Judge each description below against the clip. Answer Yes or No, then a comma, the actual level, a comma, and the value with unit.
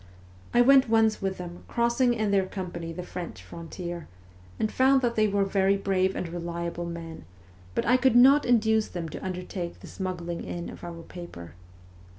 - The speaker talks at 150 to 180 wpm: Yes, average, 175 wpm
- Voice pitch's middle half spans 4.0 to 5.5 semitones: Yes, average, 4.4 semitones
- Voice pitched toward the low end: No, high, 190 Hz